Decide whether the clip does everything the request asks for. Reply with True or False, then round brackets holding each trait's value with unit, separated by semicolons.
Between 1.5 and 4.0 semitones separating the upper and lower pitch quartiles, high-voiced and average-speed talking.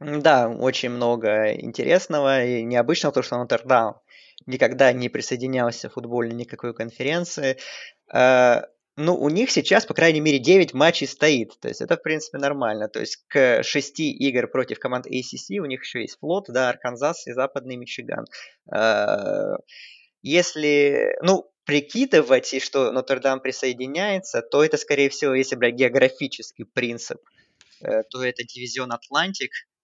False (3.6 semitones; 135 Hz; 140 wpm)